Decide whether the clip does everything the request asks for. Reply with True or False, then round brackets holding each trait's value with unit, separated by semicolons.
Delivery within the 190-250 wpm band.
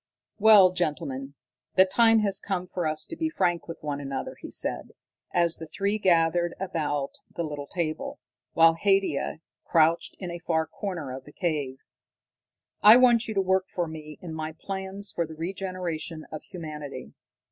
False (170 wpm)